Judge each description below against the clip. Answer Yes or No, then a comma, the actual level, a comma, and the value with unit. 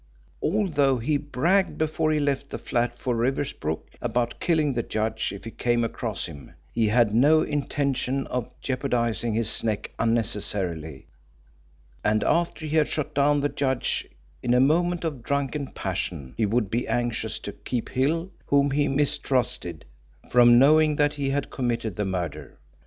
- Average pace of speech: Yes, average, 155 wpm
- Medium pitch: No, low, 125 Hz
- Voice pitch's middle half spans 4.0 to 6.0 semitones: Yes, average, 4.3 semitones